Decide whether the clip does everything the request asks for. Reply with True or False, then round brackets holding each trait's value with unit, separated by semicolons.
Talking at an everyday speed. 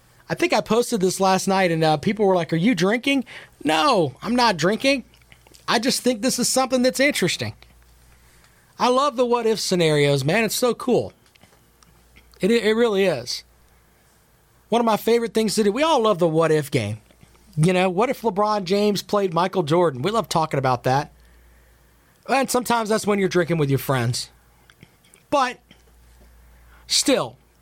True (175 wpm)